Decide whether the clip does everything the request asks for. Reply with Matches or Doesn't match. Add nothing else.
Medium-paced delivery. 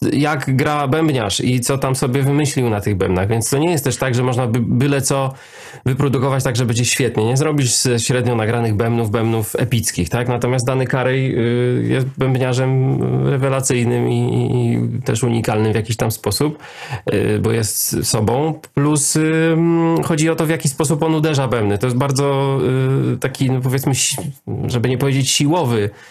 Doesn't match